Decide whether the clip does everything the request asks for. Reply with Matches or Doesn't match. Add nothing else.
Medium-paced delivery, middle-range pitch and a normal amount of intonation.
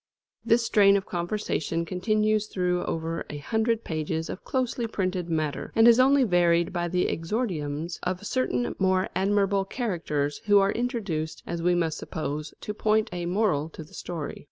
Matches